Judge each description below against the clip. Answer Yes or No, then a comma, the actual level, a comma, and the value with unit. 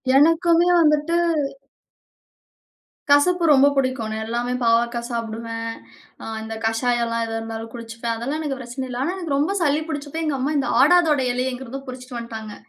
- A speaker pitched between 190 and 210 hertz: No, very high, 255 Hz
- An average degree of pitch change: Yes, average, 4.2 semitones